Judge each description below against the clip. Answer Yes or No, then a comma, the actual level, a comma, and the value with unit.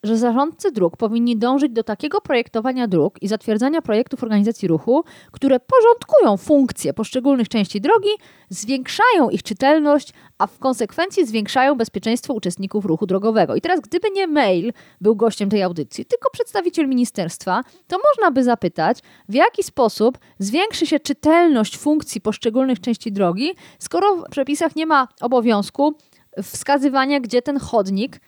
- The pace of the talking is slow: No, average, 140 wpm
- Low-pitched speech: No, very high, 250 Hz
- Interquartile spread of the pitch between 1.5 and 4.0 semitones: No, wide, 5.6 semitones